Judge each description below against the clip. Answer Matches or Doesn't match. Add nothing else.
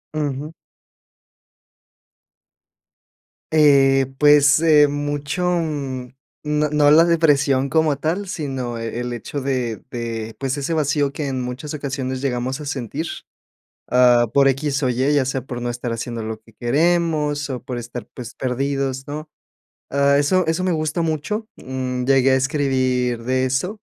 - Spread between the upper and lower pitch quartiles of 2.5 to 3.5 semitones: Matches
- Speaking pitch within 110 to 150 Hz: Matches